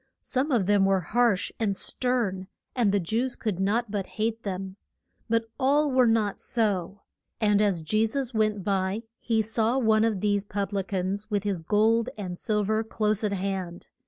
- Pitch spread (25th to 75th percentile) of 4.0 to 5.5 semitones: No, narrow, 2.6 semitones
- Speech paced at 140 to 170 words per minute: No, average, 185 wpm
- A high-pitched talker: Yes, high, 210 Hz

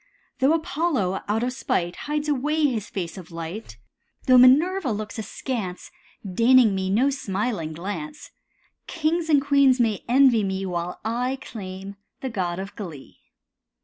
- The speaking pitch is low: No, high, 230 Hz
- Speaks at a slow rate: No, average, 145 wpm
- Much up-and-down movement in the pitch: Yes, wide, 6.3 semitones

